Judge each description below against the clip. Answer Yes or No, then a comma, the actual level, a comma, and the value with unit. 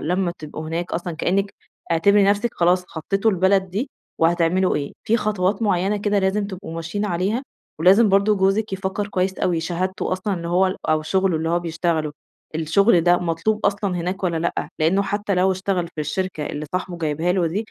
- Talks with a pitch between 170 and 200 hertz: Yes, medium, 185 Hz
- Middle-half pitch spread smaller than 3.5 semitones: Yes, average, 2.8 semitones